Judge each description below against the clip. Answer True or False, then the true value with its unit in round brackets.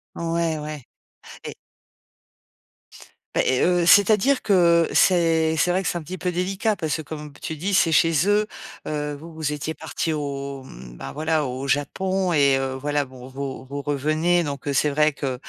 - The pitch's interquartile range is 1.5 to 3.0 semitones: False (3.6 semitones)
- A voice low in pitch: False (155 Hz)